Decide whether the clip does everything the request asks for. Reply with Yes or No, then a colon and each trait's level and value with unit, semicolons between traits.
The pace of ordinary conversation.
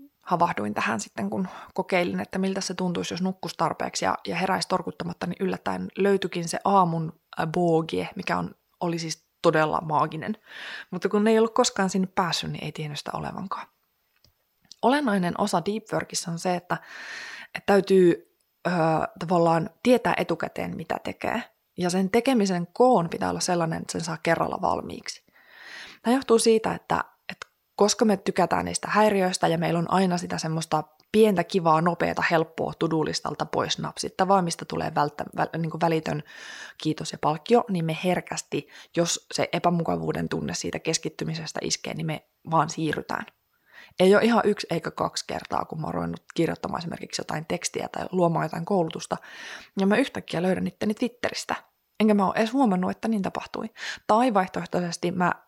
No: fast, 160 wpm